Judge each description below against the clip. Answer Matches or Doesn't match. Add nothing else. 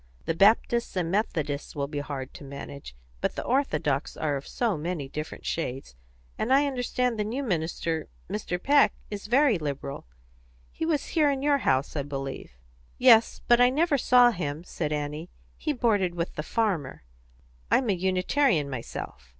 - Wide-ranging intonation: Matches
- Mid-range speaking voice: Matches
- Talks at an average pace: Matches